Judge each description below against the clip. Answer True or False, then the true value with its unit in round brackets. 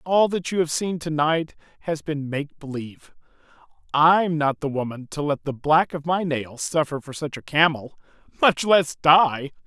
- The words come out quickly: False (185 wpm)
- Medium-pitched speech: True (150 Hz)